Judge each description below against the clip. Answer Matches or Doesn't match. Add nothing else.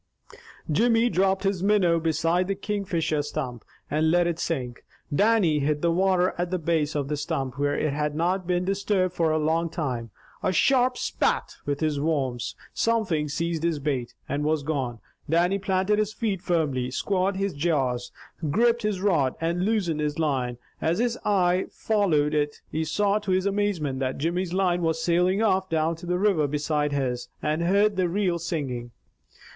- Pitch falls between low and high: Matches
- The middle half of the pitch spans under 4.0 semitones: Doesn't match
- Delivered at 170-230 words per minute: Matches